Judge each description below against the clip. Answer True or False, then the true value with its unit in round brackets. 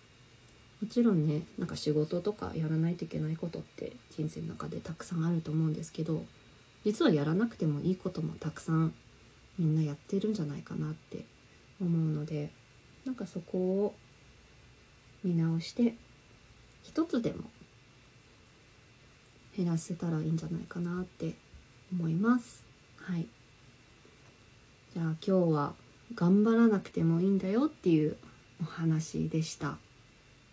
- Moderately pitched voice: True (165 Hz)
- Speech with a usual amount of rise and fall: True (3.7 semitones)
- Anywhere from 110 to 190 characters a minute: False (280 characters per minute)